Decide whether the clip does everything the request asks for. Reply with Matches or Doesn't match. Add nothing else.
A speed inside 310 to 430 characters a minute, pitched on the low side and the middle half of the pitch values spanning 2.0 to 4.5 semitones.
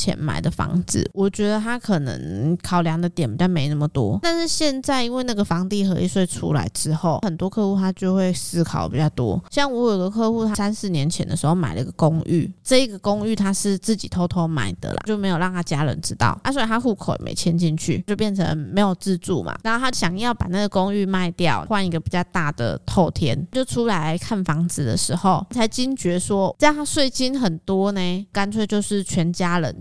Doesn't match